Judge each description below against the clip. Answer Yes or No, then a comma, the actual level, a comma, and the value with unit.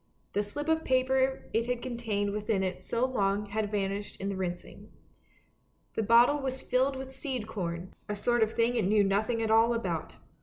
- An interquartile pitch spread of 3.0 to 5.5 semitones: Yes, average, 3.9 semitones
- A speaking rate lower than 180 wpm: No, average, 190 wpm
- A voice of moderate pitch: No, high, 225 Hz